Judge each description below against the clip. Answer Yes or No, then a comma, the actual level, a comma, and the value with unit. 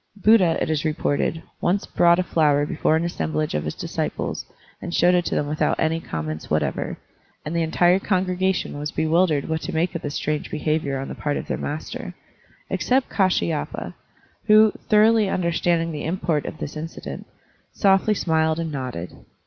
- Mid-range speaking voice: Yes, medium, 165 Hz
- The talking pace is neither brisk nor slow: Yes, average, 175 wpm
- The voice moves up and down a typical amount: Yes, average, 3.4 semitones